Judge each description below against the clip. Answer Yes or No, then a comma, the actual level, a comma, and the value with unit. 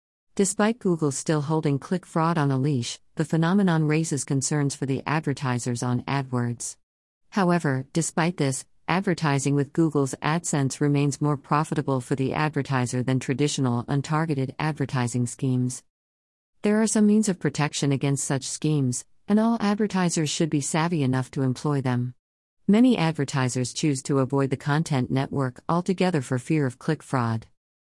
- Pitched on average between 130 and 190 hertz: Yes, medium, 140 Hz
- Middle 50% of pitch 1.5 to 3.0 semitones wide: No, average, 3.7 semitones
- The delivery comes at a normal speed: Yes, average, 150 wpm